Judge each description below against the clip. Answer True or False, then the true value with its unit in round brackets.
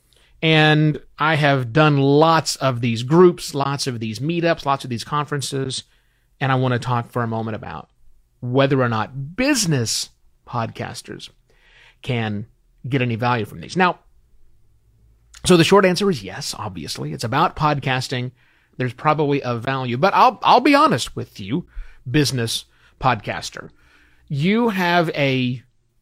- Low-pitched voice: True (130 Hz)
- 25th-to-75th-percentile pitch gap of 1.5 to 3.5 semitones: False (4.5 semitones)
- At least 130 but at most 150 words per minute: True (145 wpm)